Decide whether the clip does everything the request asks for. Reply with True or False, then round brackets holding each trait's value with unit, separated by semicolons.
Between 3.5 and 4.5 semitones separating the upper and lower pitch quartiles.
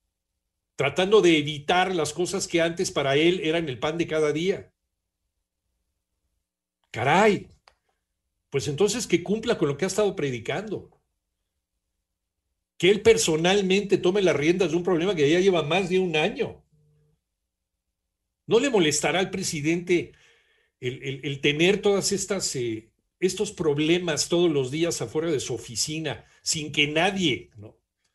False (5.1 semitones)